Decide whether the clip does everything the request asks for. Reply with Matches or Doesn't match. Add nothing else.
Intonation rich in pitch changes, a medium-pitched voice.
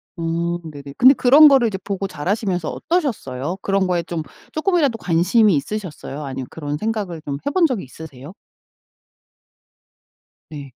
Matches